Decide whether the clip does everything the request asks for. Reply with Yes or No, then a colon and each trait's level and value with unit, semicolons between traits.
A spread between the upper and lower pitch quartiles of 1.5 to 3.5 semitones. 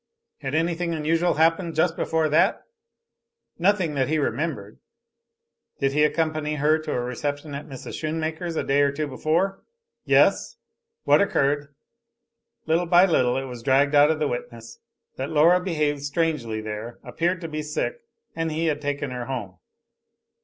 Yes: average, 2.9 semitones